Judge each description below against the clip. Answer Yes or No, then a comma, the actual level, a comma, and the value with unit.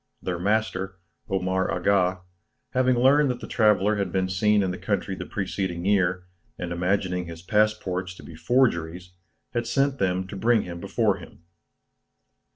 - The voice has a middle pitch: No, very low, 95 Hz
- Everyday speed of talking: Yes, average, 160 wpm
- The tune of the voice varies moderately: Yes, average, 3.1 semitones